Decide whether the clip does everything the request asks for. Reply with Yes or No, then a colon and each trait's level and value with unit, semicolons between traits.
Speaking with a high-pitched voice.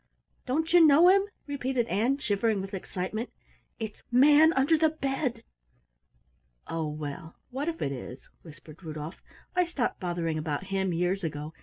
Yes: high, 215 Hz